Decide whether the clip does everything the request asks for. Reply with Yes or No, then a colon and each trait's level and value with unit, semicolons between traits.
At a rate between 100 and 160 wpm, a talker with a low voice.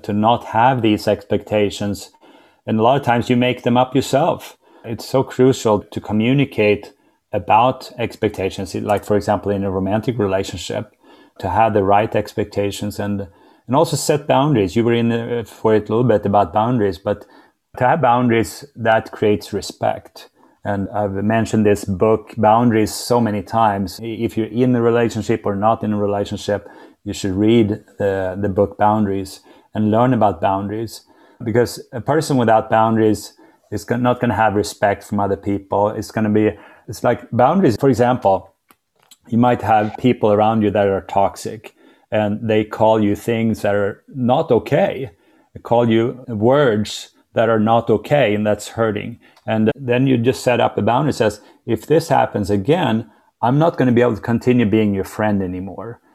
No: average, 175 wpm; low, 110 Hz